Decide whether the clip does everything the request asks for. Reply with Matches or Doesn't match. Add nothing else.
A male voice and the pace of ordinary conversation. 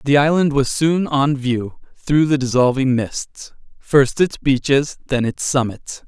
Matches